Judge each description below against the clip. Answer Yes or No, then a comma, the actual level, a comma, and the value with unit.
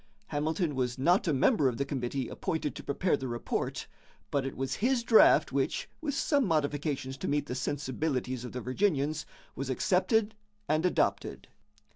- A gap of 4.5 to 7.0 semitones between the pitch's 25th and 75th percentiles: Yes, wide, 5.4 semitones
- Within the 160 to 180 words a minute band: Yes, average, 165 wpm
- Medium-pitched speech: Yes, medium, 145 Hz